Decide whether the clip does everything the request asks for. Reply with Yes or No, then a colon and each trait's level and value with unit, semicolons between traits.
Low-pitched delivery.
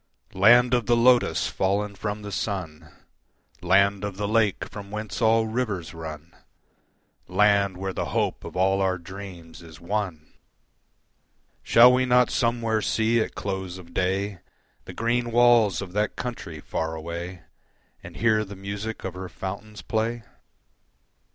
Yes: low, 100 Hz